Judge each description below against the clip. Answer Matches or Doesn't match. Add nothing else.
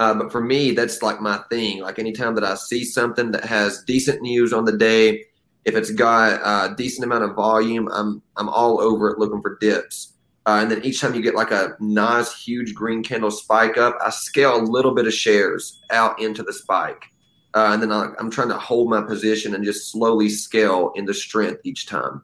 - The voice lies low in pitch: Matches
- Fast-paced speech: Matches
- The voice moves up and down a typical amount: Doesn't match